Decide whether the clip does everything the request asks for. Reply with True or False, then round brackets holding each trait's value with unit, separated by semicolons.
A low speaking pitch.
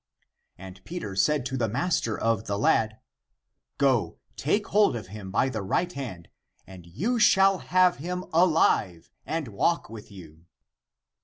True (120 Hz)